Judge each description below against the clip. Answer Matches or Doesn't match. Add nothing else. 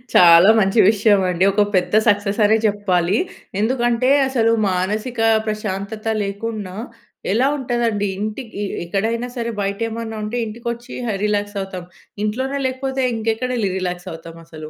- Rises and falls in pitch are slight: Doesn't match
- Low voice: Doesn't match